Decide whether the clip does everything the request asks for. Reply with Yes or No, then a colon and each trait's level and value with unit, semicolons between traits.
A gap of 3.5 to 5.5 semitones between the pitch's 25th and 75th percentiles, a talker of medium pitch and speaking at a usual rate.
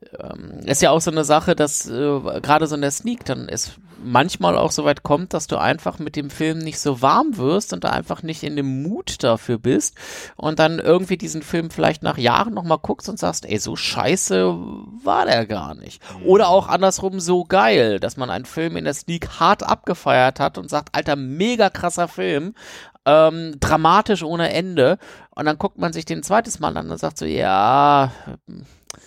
No: average, 3.9 semitones; medium, 150 Hz; fast, 200 wpm